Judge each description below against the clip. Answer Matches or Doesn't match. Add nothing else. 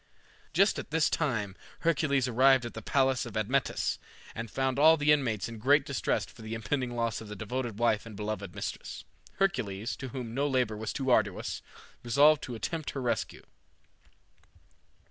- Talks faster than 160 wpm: Matches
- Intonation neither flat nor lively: Matches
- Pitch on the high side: Doesn't match